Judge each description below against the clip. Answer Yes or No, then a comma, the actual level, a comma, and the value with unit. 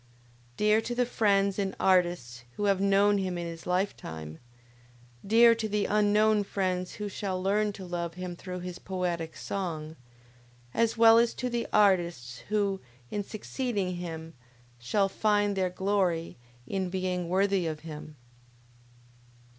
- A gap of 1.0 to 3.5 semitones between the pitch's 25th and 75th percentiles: Yes, average, 2.9 semitones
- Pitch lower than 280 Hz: Yes, high, 190 Hz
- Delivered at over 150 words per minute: No, average, 145 wpm